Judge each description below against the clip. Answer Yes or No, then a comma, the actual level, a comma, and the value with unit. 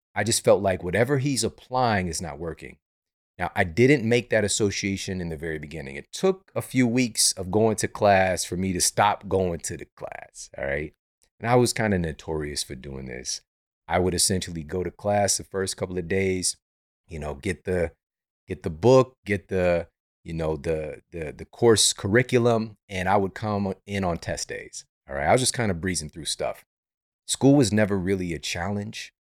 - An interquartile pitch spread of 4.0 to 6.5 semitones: Yes, average, 4.4 semitones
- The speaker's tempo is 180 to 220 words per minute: Yes, fast, 205 wpm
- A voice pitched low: Yes, very low, 95 Hz